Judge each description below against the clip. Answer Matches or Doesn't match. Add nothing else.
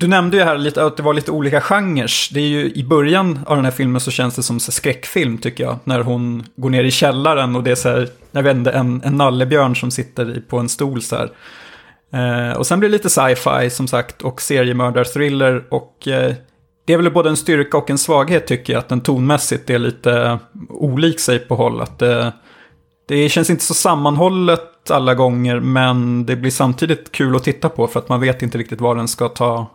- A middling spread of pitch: Matches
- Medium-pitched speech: Doesn't match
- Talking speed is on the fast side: Matches